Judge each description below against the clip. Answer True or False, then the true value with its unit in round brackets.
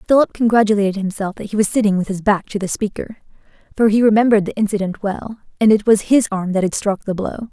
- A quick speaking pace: True (230 wpm)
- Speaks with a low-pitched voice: False (205 Hz)